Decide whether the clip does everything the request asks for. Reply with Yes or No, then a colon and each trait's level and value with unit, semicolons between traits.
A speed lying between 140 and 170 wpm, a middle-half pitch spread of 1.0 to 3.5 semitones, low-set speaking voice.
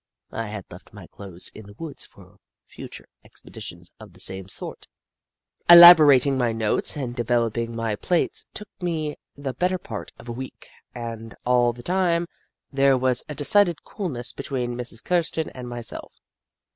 No: average, 160 wpm; average, 5.2 semitones; low, 125 Hz